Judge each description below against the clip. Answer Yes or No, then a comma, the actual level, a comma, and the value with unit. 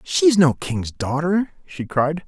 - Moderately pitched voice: Yes, medium, 150 Hz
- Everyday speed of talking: Yes, average, 185 wpm